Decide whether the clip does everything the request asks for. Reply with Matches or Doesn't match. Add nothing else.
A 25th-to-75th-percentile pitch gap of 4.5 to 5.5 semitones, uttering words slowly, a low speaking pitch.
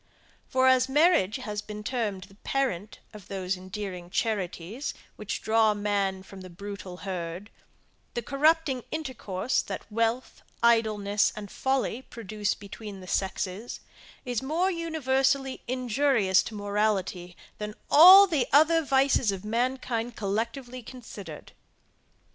Doesn't match